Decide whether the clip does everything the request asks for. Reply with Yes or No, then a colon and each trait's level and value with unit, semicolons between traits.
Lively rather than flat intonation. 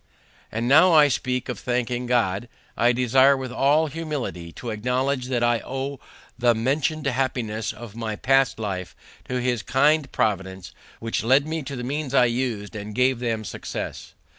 No: average, 3.0 semitones